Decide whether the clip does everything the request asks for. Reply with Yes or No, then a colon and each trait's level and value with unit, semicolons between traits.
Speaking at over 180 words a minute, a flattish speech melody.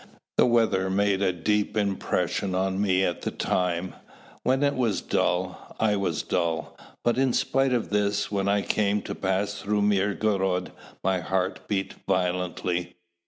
No: average, 155 wpm; narrow, 2.0 semitones